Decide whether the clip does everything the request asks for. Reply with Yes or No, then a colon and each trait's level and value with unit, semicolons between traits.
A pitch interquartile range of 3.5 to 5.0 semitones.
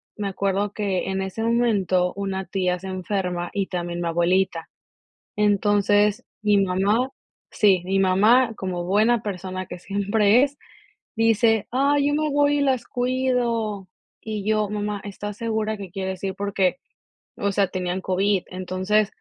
No: average, 2.8 semitones